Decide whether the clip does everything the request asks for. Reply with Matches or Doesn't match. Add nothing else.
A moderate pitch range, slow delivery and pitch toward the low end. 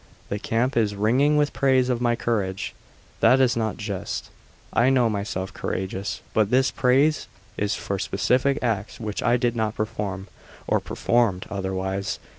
Doesn't match